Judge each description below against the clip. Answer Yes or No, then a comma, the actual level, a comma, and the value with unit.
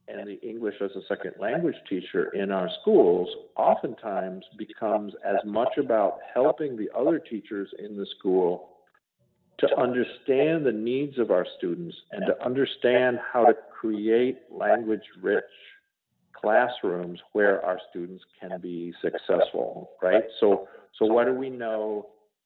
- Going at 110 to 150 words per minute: Yes, average, 140 wpm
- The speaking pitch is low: Yes, low, 115 Hz